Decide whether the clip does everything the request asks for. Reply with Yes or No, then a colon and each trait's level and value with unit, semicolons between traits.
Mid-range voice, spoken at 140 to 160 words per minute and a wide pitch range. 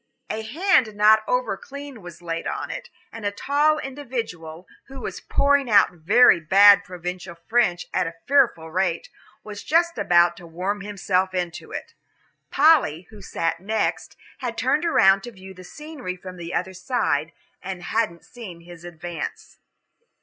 No: high, 195 Hz; average, 155 wpm; wide, 6.1 semitones